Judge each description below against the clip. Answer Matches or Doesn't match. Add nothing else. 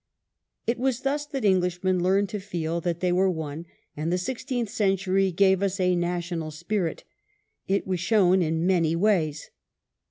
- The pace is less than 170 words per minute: Matches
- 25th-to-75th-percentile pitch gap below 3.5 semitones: Matches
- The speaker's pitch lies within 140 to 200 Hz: Matches